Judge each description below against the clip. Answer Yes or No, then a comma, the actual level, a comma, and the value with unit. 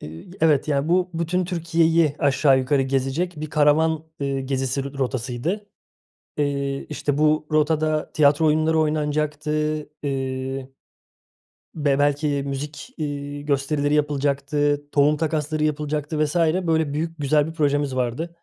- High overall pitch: No, medium, 150 Hz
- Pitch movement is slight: Yes, narrow, 2.0 semitones